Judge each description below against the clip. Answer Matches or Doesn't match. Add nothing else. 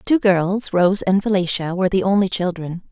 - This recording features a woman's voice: Matches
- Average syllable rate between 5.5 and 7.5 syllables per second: Matches